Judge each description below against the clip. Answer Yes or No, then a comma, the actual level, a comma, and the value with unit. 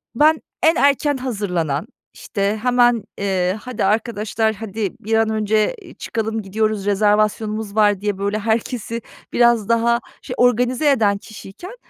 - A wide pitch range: No, average, 2.7 semitones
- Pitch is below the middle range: No, high, 220 Hz